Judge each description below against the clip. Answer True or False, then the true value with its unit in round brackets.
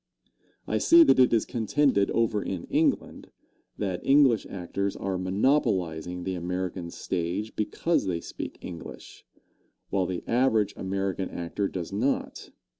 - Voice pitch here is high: False (95 Hz)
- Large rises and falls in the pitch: False (3.8 semitones)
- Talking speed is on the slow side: True (130 wpm)